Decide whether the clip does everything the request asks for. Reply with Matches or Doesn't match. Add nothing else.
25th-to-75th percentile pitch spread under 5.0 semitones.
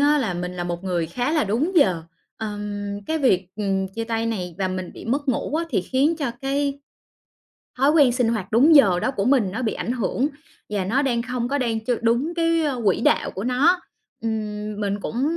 Doesn't match